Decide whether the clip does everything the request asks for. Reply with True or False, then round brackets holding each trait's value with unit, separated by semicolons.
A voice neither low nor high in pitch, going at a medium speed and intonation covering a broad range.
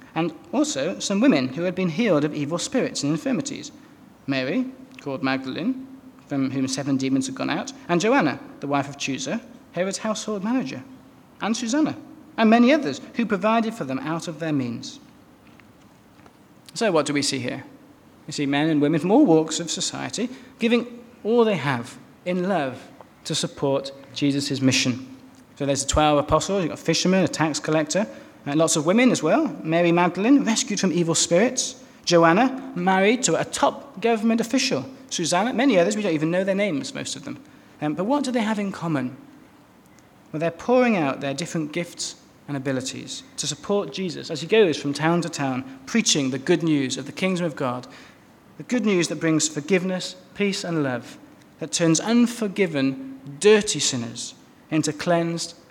True (175 Hz; 180 wpm; 8.2 semitones)